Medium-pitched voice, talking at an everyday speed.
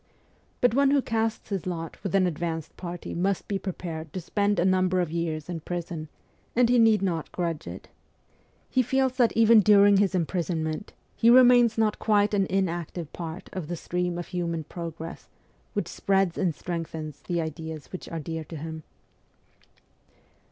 Yes: medium, 180 Hz; average, 170 wpm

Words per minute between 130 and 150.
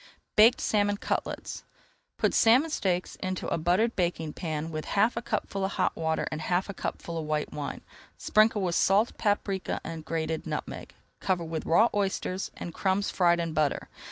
No: average, 175 wpm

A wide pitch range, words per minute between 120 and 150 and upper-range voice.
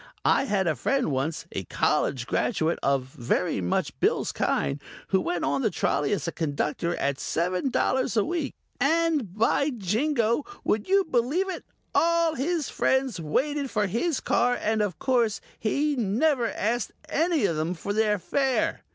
No: wide, 8.4 semitones; average, 165 wpm; high, 225 Hz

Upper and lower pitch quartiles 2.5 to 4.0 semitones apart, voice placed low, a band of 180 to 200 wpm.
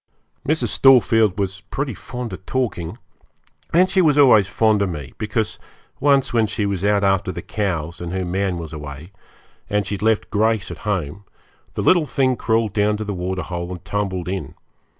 Yes: average, 3.5 semitones; low, 100 Hz; average, 185 wpm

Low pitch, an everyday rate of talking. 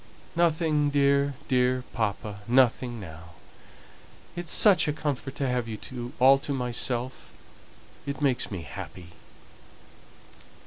No: low, 130 Hz; slow, 120 wpm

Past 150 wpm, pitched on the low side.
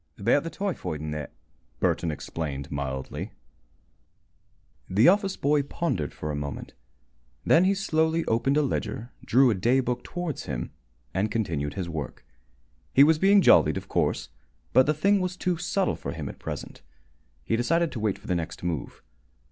Yes: average, 170 wpm; low, 120 Hz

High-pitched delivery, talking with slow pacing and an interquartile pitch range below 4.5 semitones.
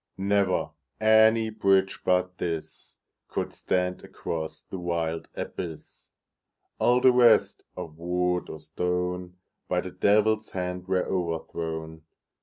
No: very low, 90 Hz; slow, 100 wpm; average, 3.0 semitones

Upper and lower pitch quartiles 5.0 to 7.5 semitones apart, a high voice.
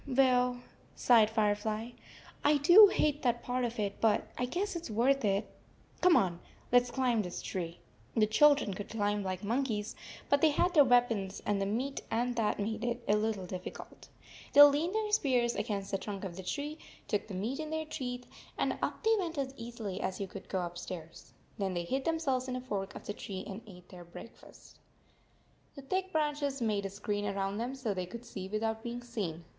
Yes: average, 5.3 semitones; high, 230 Hz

